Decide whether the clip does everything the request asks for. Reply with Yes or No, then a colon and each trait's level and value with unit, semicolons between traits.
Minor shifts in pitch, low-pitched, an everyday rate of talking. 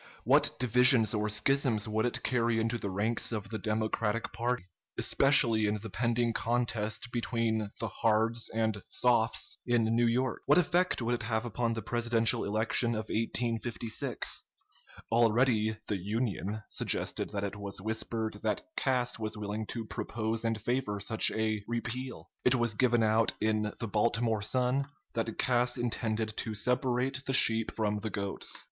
Yes: narrow, 1.9 semitones; low, 115 Hz; average, 155 wpm